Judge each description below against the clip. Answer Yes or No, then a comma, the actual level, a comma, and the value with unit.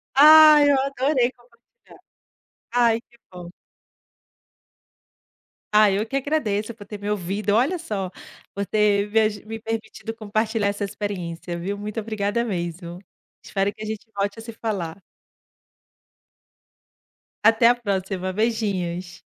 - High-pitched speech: Yes, high, 215 Hz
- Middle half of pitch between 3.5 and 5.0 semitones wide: No, average, 2.7 semitones